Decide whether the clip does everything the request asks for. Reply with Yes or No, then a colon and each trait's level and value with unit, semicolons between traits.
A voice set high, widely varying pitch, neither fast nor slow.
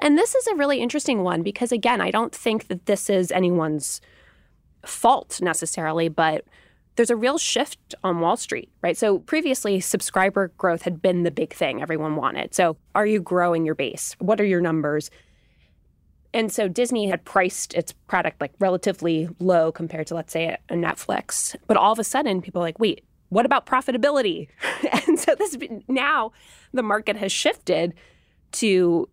Yes: high, 195 Hz; wide, 5.7 semitones; average, 175 wpm